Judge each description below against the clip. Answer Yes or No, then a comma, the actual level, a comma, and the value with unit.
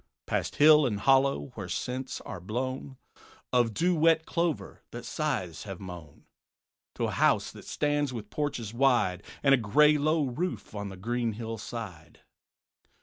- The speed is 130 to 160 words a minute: Yes, average, 150 wpm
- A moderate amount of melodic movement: No, wide, 6.2 semitones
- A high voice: No, low, 125 Hz